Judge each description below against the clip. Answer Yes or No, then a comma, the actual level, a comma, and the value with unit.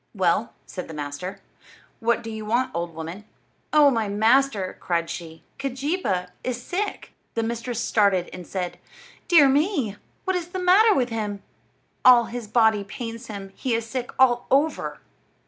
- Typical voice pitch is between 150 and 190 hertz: No, high, 230 Hz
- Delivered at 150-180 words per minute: Yes, average, 160 wpm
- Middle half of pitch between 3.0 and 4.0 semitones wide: No, average, 5.2 semitones